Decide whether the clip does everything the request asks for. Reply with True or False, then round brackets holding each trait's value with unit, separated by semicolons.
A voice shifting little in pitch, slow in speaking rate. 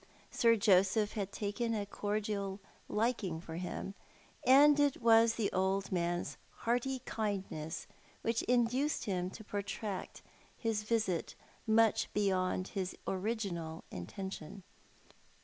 False (3.4 semitones; 115 wpm)